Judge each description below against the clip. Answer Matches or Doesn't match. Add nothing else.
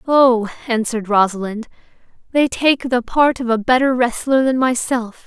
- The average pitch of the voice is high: Matches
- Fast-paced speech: Doesn't match